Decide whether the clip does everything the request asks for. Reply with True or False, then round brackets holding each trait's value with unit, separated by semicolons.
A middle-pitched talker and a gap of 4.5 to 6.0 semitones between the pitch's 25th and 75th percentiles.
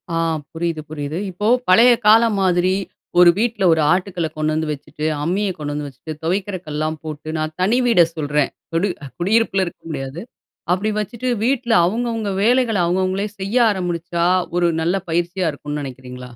True (175 Hz; 4.8 semitones)